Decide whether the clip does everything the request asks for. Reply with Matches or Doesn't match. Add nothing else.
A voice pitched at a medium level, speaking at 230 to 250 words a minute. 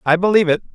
Matches